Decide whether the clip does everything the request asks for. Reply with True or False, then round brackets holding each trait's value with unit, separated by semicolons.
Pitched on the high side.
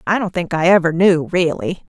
False (175 Hz)